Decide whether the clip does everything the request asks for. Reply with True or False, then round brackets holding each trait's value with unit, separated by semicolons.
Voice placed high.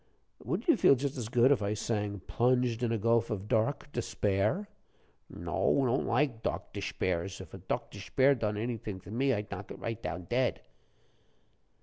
False (115 Hz)